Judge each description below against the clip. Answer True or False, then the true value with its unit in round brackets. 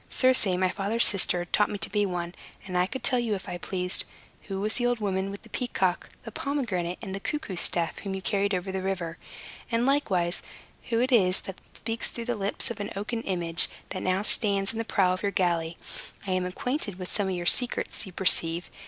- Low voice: False (195 Hz)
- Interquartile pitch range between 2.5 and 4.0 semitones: True (3.7 semitones)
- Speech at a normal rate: False (220 wpm)